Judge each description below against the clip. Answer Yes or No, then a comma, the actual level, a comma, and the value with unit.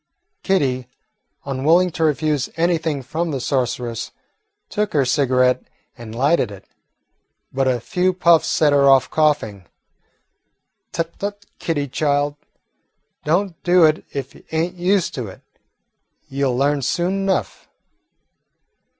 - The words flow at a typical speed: No, slow, 125 wpm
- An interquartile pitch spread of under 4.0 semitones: No, average, 4.7 semitones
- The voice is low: No, medium, 145 Hz